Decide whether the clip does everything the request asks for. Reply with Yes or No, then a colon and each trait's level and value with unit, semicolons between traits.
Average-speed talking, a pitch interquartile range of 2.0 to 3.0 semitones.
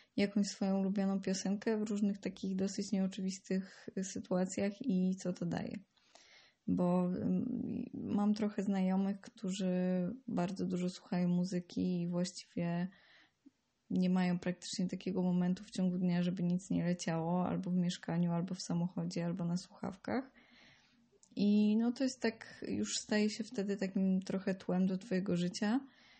Yes: average, 140 wpm; average, 2.7 semitones